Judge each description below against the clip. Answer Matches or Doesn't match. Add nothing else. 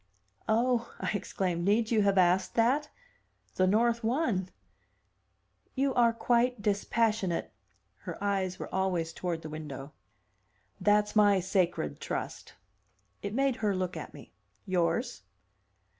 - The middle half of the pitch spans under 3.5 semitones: Doesn't match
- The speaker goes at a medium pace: Doesn't match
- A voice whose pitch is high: Matches